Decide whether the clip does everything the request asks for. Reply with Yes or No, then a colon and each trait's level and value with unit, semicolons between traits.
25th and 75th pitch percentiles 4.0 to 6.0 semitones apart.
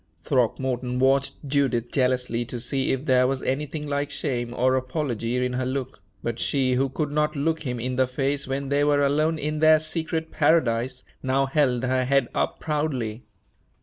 No: narrow, 2.4 semitones